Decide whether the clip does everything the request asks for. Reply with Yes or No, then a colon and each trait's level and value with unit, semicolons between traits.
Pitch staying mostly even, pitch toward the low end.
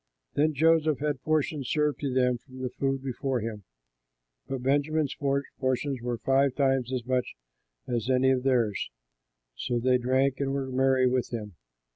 Yes: narrow, 1.8 semitones; low, 130 Hz